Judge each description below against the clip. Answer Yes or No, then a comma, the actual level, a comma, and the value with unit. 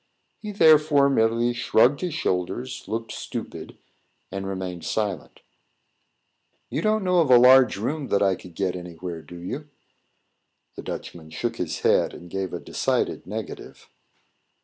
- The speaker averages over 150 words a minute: No, average, 145 wpm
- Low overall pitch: Yes, low, 115 Hz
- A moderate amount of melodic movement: No, wide, 7.4 semitones